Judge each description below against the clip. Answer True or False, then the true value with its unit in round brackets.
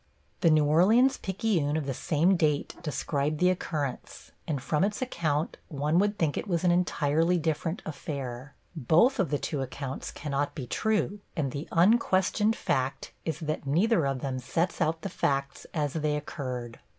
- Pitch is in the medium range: True (155 Hz)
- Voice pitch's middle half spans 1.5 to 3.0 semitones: False (4.1 semitones)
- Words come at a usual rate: True (170 wpm)